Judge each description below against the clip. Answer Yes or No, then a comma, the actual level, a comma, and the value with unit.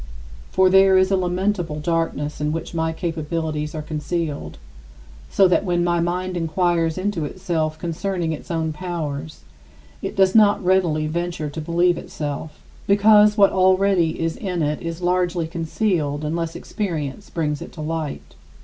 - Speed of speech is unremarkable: Yes, average, 150 wpm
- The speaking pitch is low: No, medium, 170 Hz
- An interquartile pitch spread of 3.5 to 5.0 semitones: No, average, 2.9 semitones